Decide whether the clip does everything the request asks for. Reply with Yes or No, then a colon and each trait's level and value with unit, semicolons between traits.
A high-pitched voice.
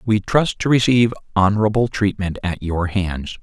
No: low, 105 Hz